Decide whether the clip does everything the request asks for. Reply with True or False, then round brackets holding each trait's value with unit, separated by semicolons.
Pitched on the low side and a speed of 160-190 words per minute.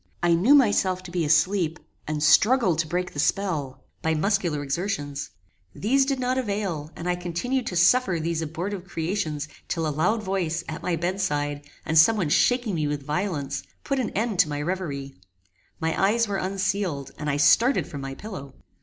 False (175 Hz; 185 wpm)